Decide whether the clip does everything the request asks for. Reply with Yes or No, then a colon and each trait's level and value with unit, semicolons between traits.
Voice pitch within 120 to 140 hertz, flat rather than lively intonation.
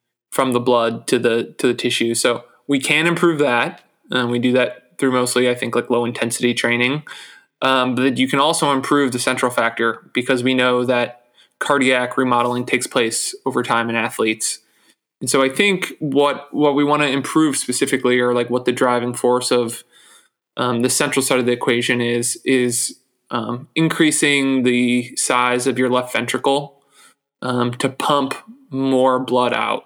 Yes: low, 125 Hz; narrow, 2.0 semitones